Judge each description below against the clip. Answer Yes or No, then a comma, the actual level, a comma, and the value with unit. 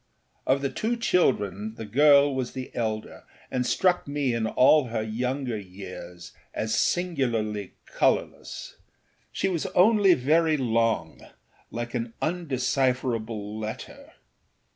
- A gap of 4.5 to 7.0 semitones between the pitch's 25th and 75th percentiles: Yes, average, 5.1 semitones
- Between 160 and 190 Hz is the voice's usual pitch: No, low, 125 Hz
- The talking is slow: Yes, slow, 120 wpm